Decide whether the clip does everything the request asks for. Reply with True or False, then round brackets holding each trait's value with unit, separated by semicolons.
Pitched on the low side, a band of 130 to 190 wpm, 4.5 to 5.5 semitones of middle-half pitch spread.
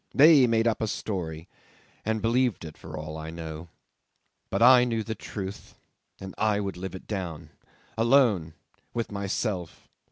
True (100 Hz; 155 wpm; 5.2 semitones)